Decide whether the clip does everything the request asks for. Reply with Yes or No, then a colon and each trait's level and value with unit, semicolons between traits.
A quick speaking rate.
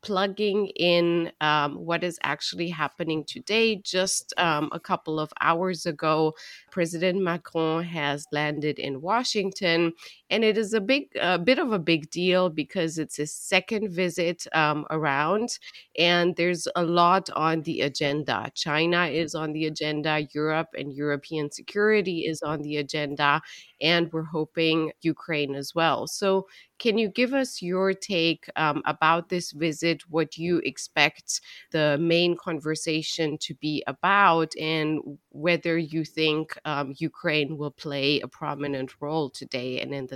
No: average, 150 wpm